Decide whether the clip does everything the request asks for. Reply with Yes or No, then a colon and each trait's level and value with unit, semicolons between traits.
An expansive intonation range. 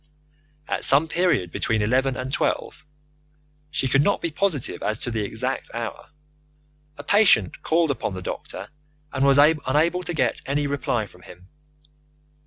Yes: wide, 5.8 semitones